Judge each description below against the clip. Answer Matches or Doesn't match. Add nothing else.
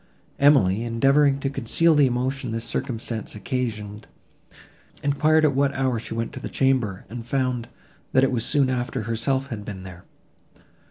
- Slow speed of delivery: Doesn't match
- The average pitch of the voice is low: Matches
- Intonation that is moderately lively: Matches